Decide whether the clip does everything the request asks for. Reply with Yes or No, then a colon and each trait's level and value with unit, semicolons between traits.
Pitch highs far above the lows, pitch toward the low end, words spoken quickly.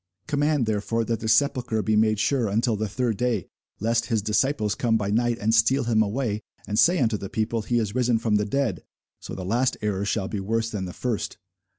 No: narrow, 2.4 semitones; low, 110 Hz; fast, 220 wpm